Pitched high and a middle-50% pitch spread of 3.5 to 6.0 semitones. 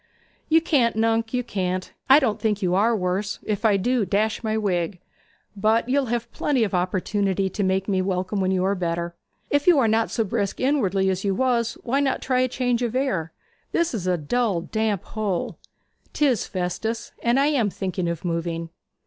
Yes: high, 210 Hz; average, 4.4 semitones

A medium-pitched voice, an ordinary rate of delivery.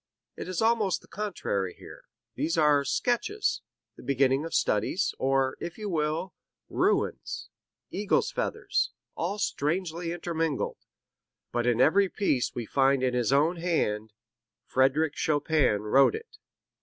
No: medium, 155 Hz; slow, 130 wpm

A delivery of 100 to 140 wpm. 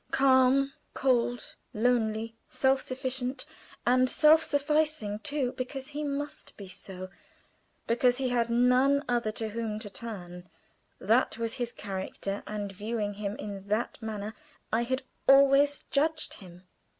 Yes: slow, 135 wpm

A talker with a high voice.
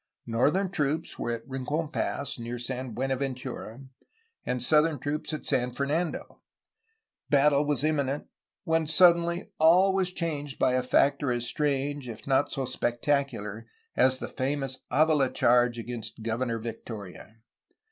No: low, 135 Hz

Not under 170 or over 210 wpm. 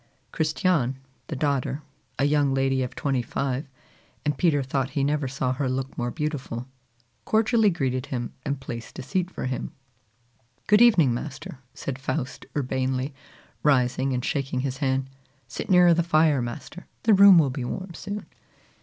No: average, 160 wpm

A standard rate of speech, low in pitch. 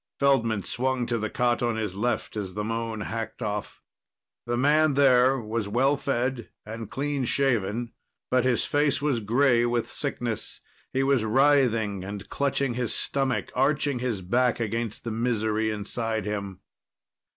Yes: average, 150 wpm; low, 120 Hz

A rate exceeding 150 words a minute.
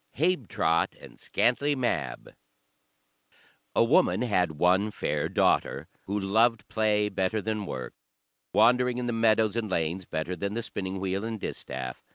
No: average, 145 wpm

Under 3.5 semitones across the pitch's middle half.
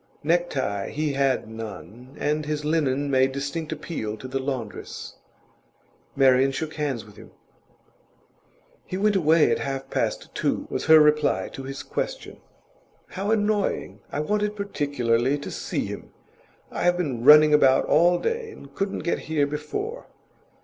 No: average, 4.2 semitones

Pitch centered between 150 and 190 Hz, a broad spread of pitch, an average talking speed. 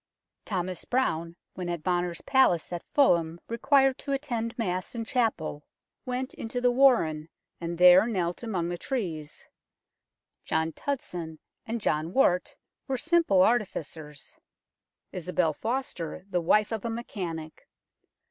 No: medium, 185 Hz; wide, 6.3 semitones; slow, 130 wpm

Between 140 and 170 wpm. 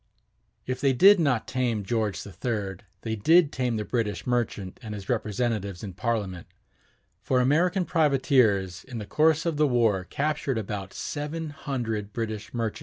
Yes: average, 155 wpm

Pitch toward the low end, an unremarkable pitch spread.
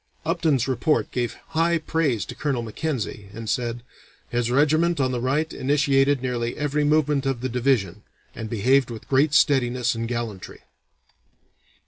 Yes: low, 130 Hz; average, 3.8 semitones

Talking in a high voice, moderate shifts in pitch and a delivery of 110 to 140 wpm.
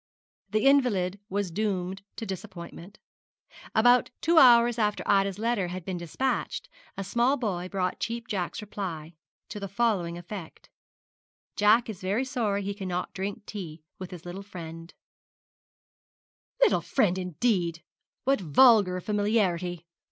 Yes: high, 195 Hz; average, 3.8 semitones; slow, 135 wpm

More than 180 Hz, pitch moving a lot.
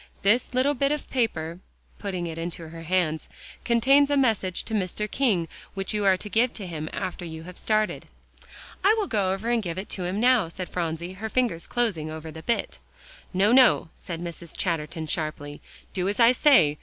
Yes: high, 190 Hz; wide, 5.9 semitones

